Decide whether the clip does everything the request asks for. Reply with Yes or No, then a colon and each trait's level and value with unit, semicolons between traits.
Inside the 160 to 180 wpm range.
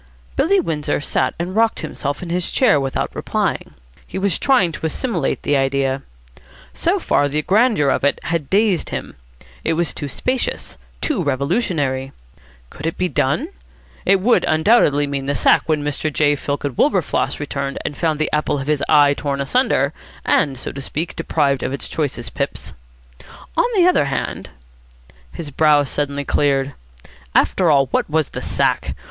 Yes: average, 165 wpm